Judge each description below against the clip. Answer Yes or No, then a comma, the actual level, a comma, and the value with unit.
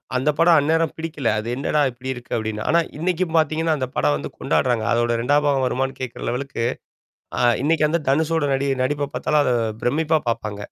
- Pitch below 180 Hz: Yes, medium, 140 Hz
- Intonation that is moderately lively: Yes, average, 4.5 semitones